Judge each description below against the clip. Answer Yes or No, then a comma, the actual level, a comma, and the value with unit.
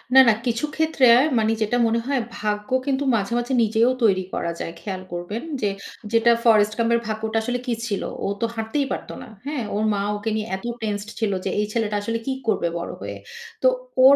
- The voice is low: No, high, 220 Hz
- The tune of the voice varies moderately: No, narrow, 2.3 semitones